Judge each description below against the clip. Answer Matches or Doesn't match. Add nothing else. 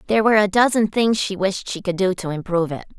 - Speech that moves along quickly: Matches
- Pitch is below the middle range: Doesn't match